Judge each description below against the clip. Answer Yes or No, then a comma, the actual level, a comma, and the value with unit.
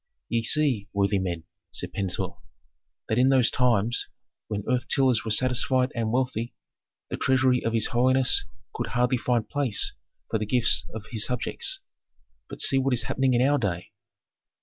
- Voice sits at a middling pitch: No, low, 120 Hz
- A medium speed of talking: Yes, average, 165 wpm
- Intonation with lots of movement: No, average, 2.9 semitones